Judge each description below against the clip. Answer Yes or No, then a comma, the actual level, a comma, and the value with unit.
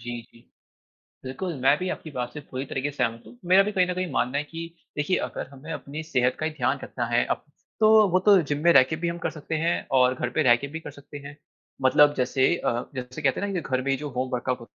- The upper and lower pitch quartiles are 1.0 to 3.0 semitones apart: No, average, 4.3 semitones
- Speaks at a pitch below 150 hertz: Yes, medium, 140 Hz